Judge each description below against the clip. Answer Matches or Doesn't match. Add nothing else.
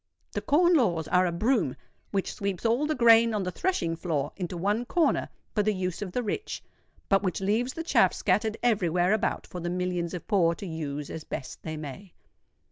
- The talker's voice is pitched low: Doesn't match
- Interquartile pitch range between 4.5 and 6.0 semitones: Matches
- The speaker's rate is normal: Doesn't match